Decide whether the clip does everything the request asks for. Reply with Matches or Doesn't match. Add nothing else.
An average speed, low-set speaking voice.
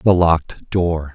Matches